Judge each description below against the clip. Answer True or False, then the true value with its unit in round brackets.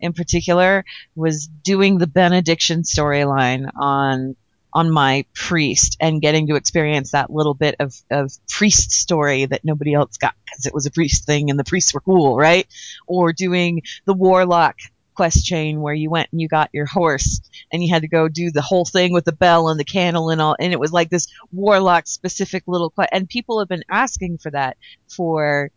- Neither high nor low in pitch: True (160 Hz)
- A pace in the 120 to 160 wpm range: False (200 wpm)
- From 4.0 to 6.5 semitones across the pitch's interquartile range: False (3.5 semitones)